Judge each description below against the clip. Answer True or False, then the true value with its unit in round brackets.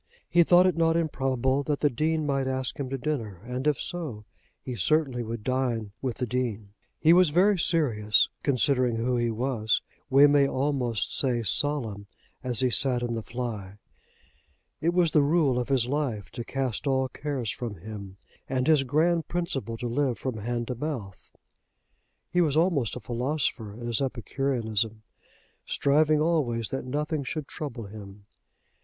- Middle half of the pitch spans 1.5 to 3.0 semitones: False (4.2 semitones)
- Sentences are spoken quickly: False (165 wpm)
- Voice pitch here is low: True (130 Hz)